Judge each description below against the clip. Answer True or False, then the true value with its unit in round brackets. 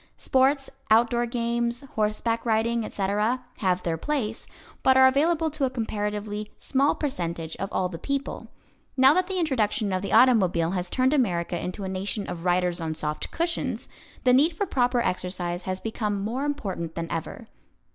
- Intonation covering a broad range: True (6.1 semitones)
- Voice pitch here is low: False (220 Hz)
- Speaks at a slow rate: False (165 wpm)